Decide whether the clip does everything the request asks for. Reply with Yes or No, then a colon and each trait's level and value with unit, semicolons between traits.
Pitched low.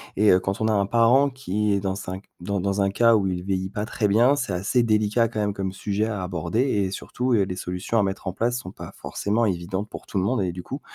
Yes: low, 100 Hz